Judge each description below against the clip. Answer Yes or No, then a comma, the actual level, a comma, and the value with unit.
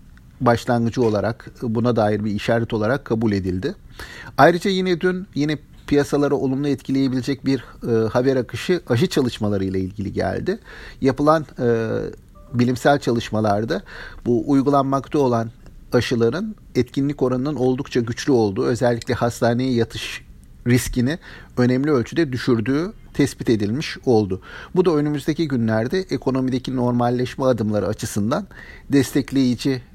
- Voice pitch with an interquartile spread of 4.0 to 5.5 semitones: No, average, 3.5 semitones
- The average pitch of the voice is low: Yes, low, 125 Hz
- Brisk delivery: No, average, 115 wpm